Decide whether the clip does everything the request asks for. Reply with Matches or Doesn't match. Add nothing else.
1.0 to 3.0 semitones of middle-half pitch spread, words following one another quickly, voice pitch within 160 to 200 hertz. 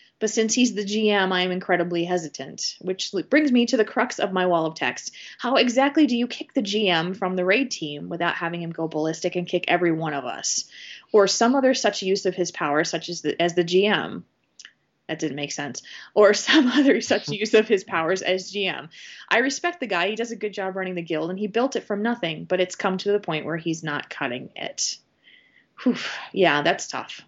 Doesn't match